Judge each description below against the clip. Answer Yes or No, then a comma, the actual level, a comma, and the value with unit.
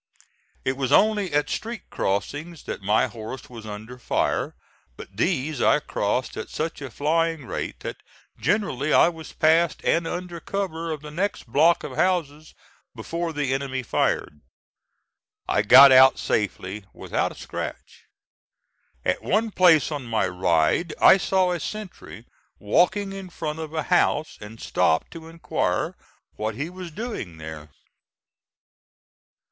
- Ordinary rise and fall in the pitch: No, wide, 6.6 semitones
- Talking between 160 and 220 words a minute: No, average, 145 wpm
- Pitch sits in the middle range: Yes, medium, 150 Hz